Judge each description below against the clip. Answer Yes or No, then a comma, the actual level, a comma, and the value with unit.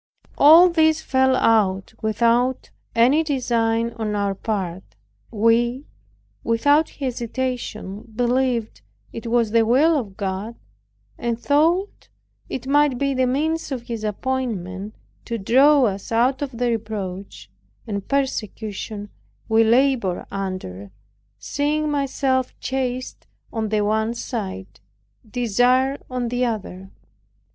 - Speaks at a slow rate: Yes, slow, 115 wpm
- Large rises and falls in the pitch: No, average, 3.8 semitones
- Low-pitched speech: No, high, 235 Hz